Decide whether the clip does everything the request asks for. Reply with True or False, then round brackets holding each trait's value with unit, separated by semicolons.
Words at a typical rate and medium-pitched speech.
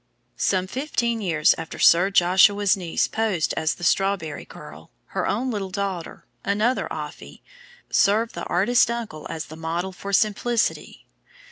False (145 wpm; 195 Hz)